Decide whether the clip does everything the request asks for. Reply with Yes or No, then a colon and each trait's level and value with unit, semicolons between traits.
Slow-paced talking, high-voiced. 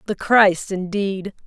Yes: slow, 125 wpm; high, 195 Hz